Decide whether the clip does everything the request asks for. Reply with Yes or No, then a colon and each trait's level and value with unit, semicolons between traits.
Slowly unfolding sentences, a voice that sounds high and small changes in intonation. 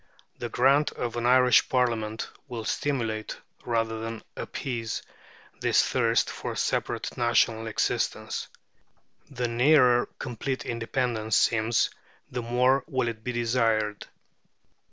No: slow, 115 wpm; low, 120 Hz; narrow, 1.9 semitones